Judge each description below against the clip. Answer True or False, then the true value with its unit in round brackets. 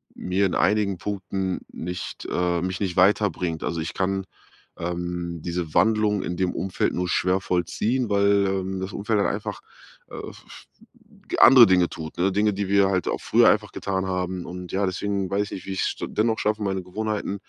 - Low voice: True (95 Hz)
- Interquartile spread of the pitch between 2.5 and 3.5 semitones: False (2.1 semitones)